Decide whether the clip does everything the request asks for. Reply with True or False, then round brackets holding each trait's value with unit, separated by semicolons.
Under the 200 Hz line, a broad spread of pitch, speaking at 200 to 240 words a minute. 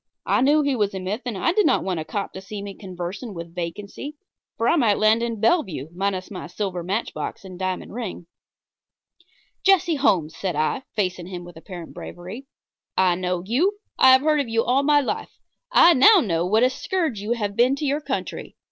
False (205 Hz; 6.5 semitones; 205 wpm)